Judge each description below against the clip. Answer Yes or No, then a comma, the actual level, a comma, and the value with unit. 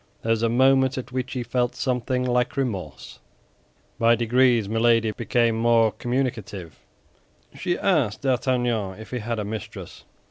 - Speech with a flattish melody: Yes, narrow, 2.3 semitones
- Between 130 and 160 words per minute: Yes, average, 145 wpm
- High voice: No, low, 120 Hz